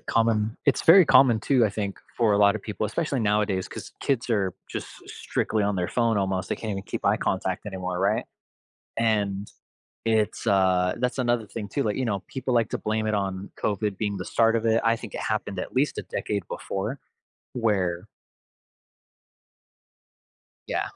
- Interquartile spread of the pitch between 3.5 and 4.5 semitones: No, average, 2.8 semitones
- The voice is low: Yes, low, 105 Hz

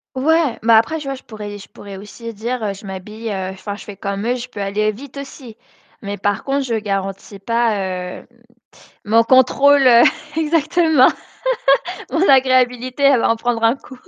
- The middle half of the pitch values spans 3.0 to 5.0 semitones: Yes, average, 4.4 semitones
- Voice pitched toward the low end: No, high, 230 Hz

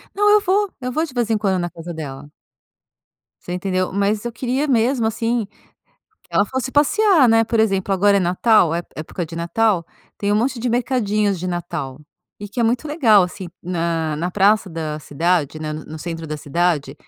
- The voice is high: Yes, high, 200 Hz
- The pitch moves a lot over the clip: Yes, wide, 5.9 semitones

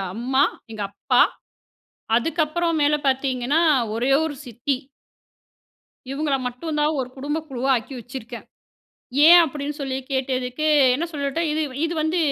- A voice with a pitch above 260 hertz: Yes, very high, 275 Hz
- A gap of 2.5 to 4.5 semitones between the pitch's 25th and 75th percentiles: Yes, average, 3.4 semitones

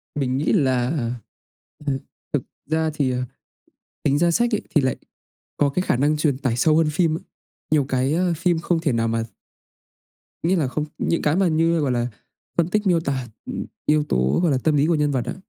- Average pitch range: Yes, average, 4.1 semitones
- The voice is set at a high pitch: No, medium, 150 Hz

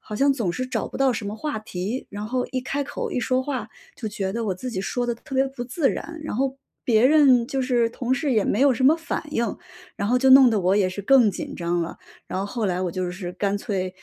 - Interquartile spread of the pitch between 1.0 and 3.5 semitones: No, average, 4.8 semitones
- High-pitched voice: Yes, high, 240 Hz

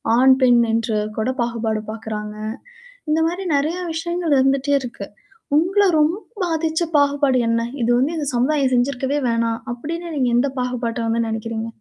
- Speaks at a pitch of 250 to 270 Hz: Yes, very high, 260 Hz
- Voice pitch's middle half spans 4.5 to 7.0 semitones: Yes, average, 4.8 semitones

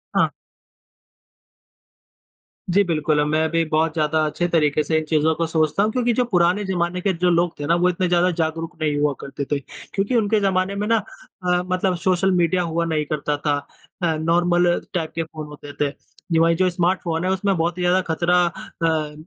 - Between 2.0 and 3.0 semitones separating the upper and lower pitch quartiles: Yes, narrow, 2.6 semitones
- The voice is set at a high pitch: No, medium, 170 Hz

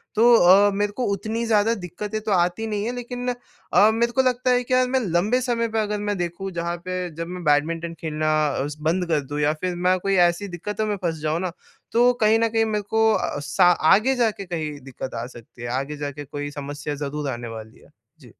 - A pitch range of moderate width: No, wide, 6.4 semitones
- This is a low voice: No, medium, 185 Hz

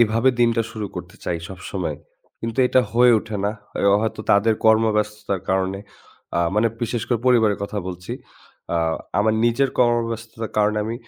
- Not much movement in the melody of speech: Yes, narrow, 2.0 semitones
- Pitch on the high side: No, low, 110 Hz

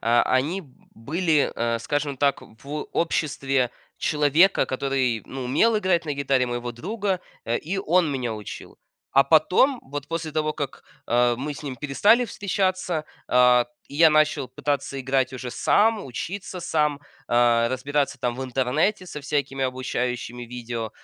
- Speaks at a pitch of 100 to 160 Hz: Yes, medium, 140 Hz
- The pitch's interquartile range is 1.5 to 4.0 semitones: No, average, 4.4 semitones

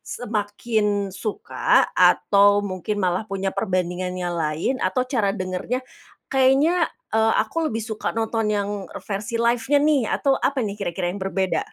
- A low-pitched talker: No, high, 205 Hz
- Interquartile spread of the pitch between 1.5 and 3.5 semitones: No, average, 4.1 semitones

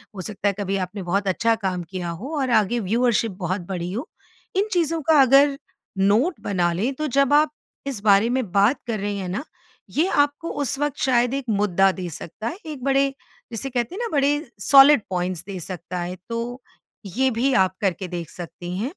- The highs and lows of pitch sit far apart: Yes, wide, 6.5 semitones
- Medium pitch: No, high, 220 Hz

